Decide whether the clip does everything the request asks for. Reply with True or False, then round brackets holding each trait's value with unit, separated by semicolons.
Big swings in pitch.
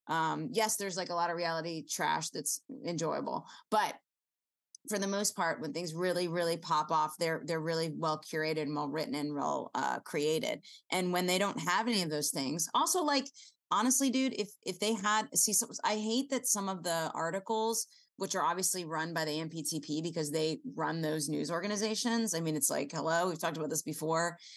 False (4.8 semitones)